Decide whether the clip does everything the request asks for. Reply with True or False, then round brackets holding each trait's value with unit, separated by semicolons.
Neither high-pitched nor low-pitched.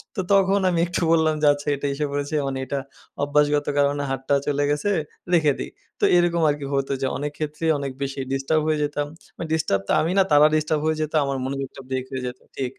True (145 Hz)